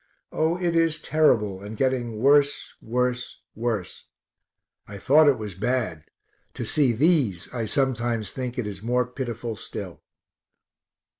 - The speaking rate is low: Yes, slow, 130 wpm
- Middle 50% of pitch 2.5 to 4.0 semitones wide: No, average, 4.4 semitones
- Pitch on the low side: Yes, low, 125 Hz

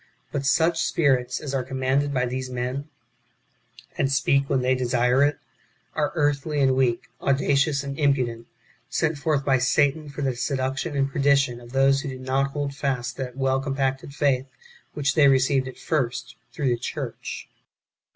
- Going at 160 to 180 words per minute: Yes, average, 170 wpm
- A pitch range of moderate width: No, narrow, 1.6 semitones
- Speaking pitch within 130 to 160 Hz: Yes, low, 135 Hz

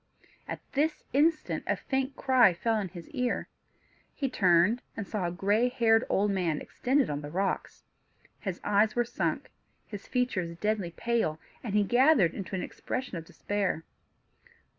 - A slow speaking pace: No, average, 155 wpm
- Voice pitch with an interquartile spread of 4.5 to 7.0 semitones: Yes, average, 5.3 semitones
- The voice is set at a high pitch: Yes, high, 210 Hz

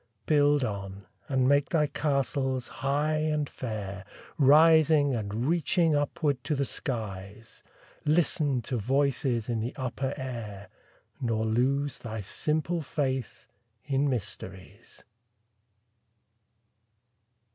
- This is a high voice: No, low, 135 Hz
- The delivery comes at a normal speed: No, slow, 105 wpm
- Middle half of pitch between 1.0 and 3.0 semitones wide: No, average, 4.6 semitones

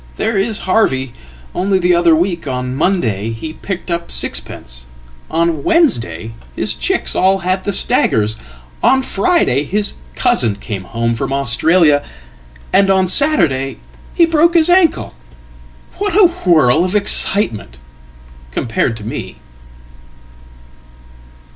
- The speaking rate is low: Yes, slow, 110 wpm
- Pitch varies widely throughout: Yes, wide, 8.8 semitones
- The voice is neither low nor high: Yes, medium, 170 Hz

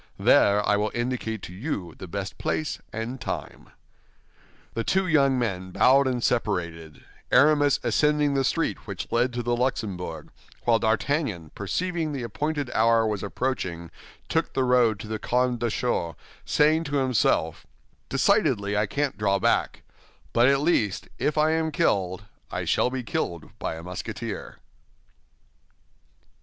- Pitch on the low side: Yes, low, 120 Hz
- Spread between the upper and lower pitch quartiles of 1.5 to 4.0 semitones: No, wide, 5.5 semitones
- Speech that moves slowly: No, average, 145 wpm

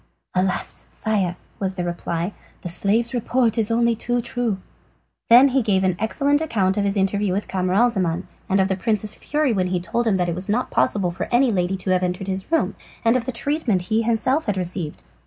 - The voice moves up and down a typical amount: Yes, average, 4.2 semitones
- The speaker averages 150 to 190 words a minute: No, average, 200 wpm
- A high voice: Yes, high, 205 Hz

